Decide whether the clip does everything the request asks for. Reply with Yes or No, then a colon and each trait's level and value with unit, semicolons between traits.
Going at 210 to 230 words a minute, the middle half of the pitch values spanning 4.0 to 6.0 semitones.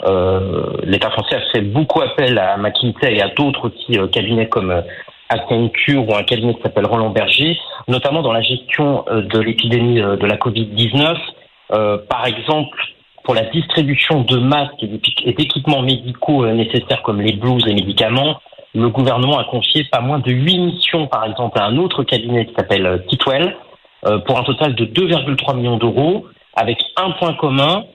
No: average, 190 wpm; average, 4.6 semitones